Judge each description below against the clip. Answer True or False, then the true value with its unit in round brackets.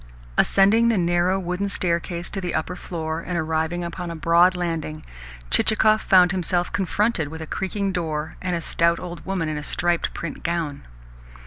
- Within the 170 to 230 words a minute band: True (175 wpm)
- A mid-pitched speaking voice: True (175 Hz)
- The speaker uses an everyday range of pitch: False (2.2 semitones)